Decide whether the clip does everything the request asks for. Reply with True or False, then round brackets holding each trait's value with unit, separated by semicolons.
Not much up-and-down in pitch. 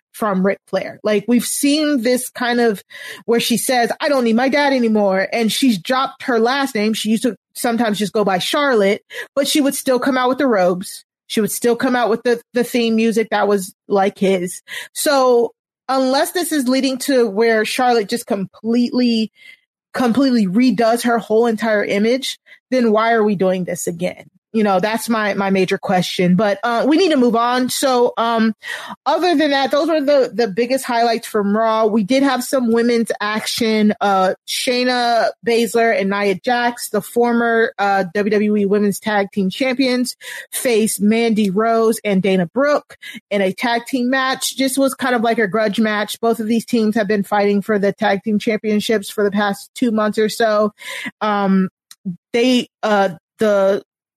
False (3.3 semitones)